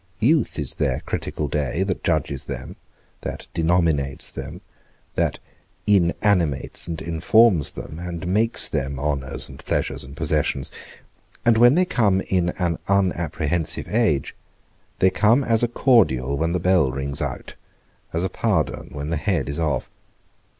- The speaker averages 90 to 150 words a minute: Yes, average, 145 wpm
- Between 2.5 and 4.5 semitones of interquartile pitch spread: No, wide, 5.4 semitones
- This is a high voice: No, very low, 85 Hz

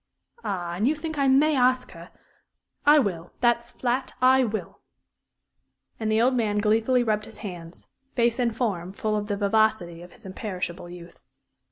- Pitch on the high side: Yes, high, 220 Hz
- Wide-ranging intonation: No, average, 4.8 semitones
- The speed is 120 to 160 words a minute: No, average, 170 wpm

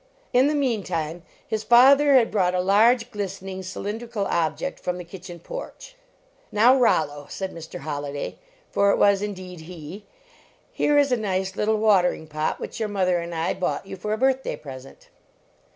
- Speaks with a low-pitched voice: No, high, 195 Hz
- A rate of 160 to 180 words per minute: Yes, average, 170 wpm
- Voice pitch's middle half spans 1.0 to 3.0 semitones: No, average, 4.8 semitones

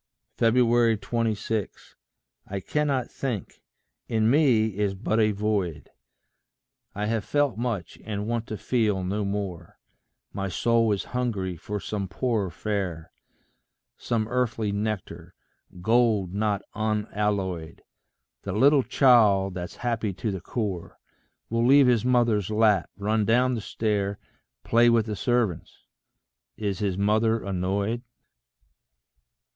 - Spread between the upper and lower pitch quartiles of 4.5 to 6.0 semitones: No, average, 2.9 semitones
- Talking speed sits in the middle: No, slow, 120 wpm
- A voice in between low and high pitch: No, low, 105 Hz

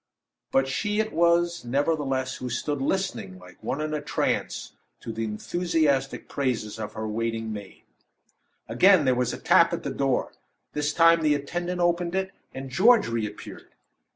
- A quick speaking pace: No, average, 160 wpm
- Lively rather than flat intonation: Yes, wide, 6.8 semitones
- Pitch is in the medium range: Yes, medium, 145 Hz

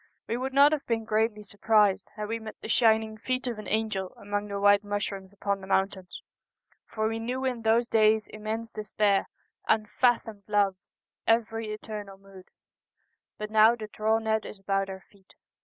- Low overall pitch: No, high, 215 Hz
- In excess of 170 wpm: Yes, average, 185 wpm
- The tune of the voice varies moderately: No, narrow, 1.8 semitones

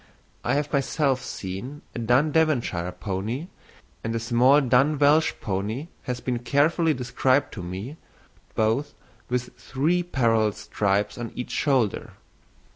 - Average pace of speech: No, slow, 130 wpm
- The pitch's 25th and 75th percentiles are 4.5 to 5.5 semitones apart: Yes, average, 4.8 semitones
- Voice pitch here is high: No, low, 125 Hz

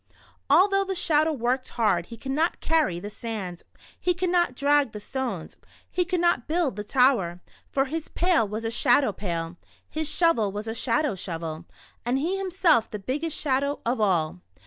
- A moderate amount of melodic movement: No, wide, 7.4 semitones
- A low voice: No, very high, 260 Hz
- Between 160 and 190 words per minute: Yes, average, 180 wpm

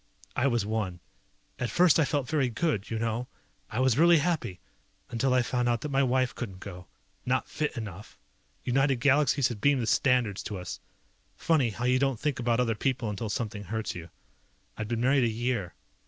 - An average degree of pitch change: Yes, average, 3.6 semitones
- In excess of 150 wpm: Yes, average, 195 wpm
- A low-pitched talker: Yes, low, 120 Hz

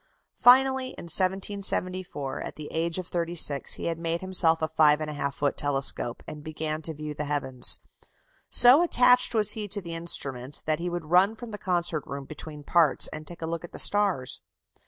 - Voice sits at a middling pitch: Yes, medium, 165 Hz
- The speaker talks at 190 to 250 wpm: Yes, average, 200 wpm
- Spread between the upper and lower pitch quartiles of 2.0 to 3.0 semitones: No, average, 4.0 semitones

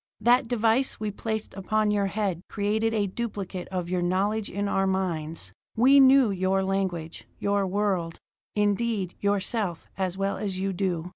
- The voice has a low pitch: No, high, 200 Hz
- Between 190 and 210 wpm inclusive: No, average, 155 wpm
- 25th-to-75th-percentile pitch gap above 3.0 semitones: No, narrow, 2.6 semitones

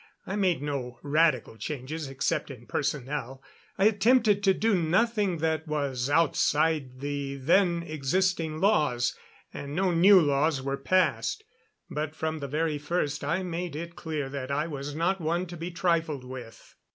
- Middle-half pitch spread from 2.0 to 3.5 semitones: No, average, 3.9 semitones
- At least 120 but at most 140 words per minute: No, average, 155 wpm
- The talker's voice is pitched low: No, medium, 155 Hz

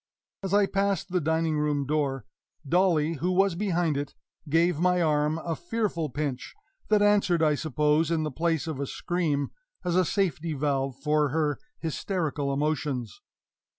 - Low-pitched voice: No, medium, 160 Hz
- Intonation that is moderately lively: Yes, average, 3.2 semitones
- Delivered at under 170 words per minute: Yes, average, 155 wpm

